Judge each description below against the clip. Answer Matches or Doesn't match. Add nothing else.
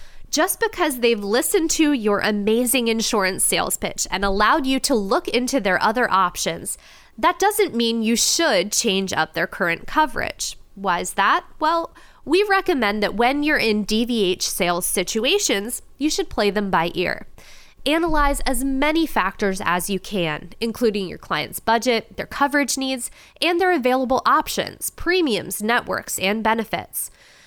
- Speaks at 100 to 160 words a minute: Matches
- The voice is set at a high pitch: Matches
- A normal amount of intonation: Doesn't match